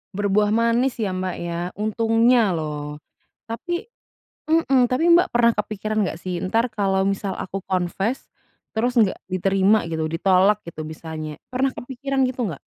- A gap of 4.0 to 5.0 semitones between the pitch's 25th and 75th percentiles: Yes, average, 4.5 semitones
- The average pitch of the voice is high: Yes, high, 205 Hz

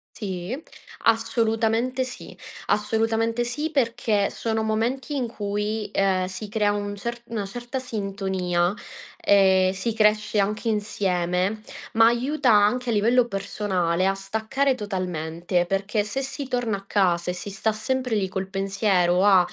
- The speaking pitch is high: Yes, high, 210 Hz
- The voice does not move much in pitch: No, average, 3.1 semitones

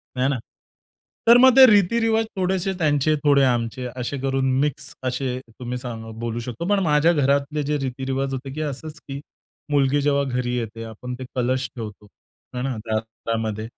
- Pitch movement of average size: Yes, average, 3.2 semitones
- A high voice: No, low, 135 Hz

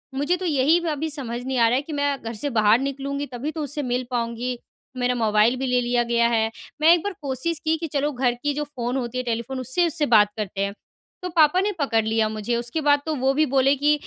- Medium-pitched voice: No, very high, 265 Hz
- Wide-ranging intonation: No, average, 3.7 semitones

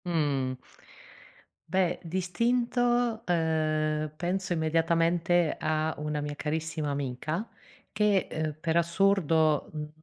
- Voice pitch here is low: No, medium, 160 Hz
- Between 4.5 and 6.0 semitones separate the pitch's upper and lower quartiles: No, average, 2.9 semitones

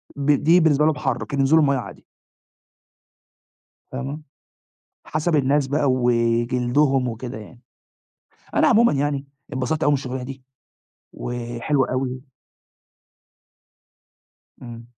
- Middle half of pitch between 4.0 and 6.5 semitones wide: No, average, 3.1 semitones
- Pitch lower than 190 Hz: Yes, low, 135 Hz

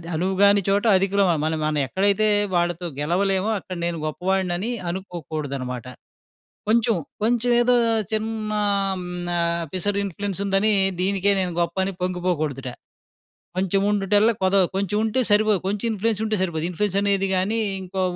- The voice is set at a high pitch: Yes, high, 195 Hz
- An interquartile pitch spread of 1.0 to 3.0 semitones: Yes, narrow, 2.6 semitones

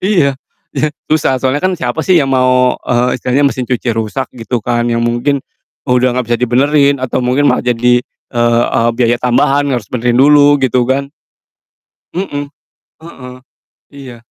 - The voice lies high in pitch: No, low, 125 Hz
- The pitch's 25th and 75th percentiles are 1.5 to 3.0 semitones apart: Yes, average, 2.7 semitones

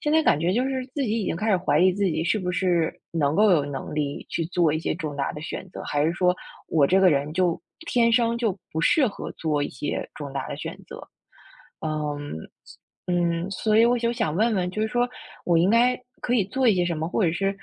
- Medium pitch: Yes, medium, 180 Hz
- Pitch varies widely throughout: Yes, wide, 5.9 semitones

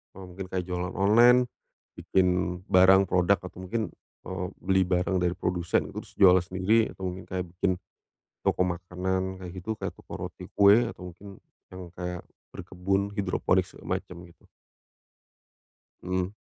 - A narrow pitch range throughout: Yes, narrow, 1.3 semitones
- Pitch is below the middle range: Yes, very low, 95 Hz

